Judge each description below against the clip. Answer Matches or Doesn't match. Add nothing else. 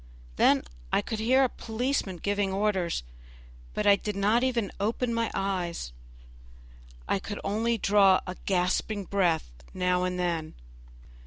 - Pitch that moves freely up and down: Doesn't match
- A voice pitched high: Matches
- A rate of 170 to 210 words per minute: Doesn't match